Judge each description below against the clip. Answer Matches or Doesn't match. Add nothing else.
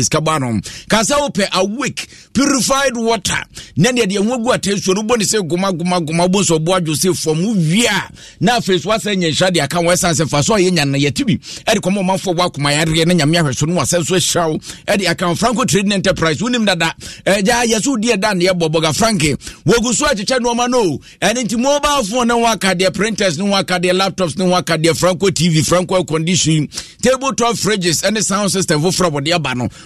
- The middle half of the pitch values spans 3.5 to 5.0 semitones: Matches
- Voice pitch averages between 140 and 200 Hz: Matches